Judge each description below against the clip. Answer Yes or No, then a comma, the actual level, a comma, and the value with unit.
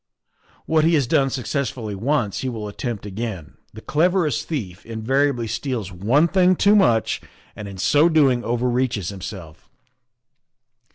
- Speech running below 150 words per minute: No, average, 155 wpm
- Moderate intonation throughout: No, wide, 5.7 semitones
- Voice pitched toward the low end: Yes, low, 120 Hz